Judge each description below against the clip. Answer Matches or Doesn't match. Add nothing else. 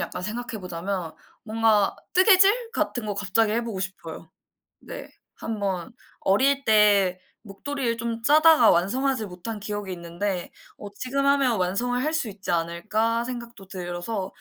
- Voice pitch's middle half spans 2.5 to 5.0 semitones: Matches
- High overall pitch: Matches